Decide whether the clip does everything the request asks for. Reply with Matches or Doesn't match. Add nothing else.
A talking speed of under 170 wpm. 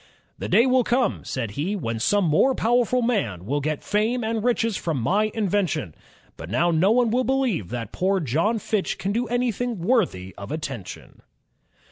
Doesn't match